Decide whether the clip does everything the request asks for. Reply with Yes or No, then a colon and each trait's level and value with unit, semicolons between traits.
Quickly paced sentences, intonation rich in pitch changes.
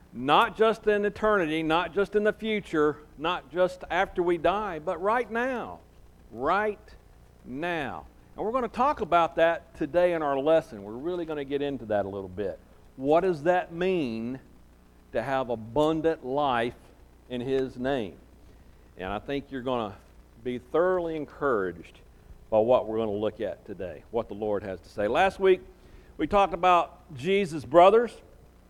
No: average, 170 wpm; wide, 7.9 semitones